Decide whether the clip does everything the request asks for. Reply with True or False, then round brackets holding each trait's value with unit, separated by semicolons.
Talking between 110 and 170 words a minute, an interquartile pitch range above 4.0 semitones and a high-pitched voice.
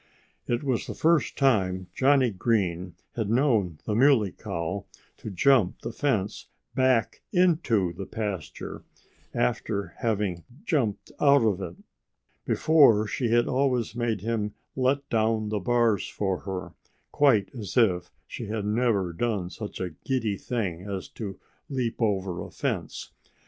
False (140 wpm; 4.6 semitones; 110 Hz)